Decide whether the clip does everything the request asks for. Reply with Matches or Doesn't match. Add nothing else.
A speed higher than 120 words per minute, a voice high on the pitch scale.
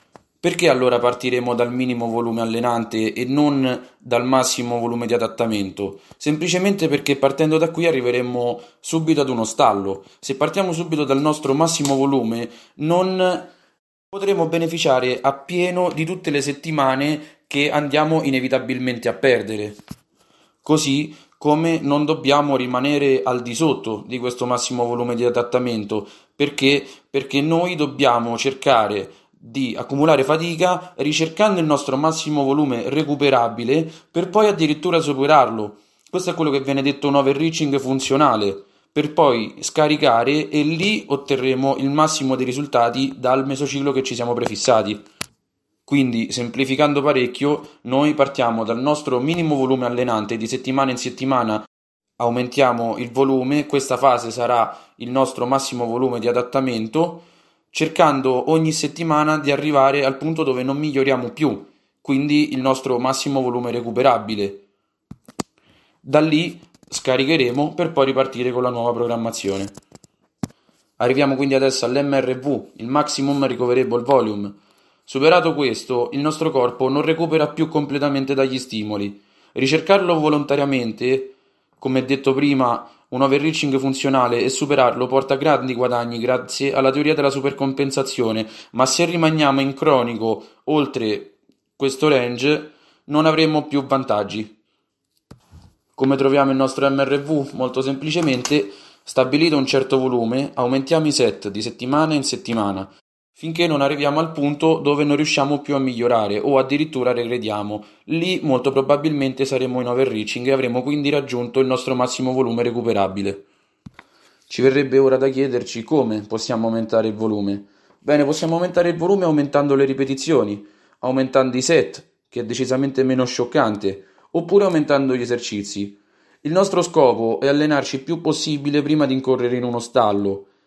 Doesn't match